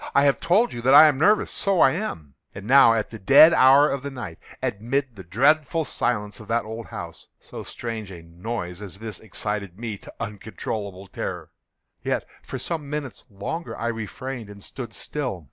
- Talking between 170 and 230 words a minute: Yes, average, 190 wpm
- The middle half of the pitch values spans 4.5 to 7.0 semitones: Yes, wide, 5.5 semitones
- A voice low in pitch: Yes, low, 115 Hz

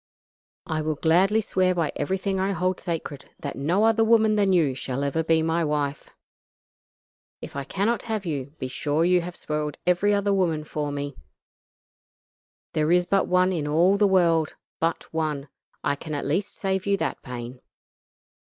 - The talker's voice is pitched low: No, medium, 165 Hz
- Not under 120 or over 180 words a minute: Yes, average, 170 wpm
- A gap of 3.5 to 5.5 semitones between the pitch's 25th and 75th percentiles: Yes, average, 4.4 semitones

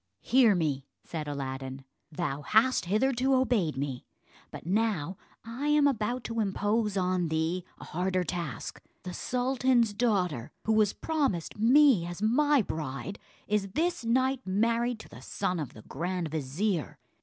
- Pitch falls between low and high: No, high, 200 Hz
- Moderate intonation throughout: No, wide, 6.9 semitones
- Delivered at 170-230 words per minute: No, average, 145 wpm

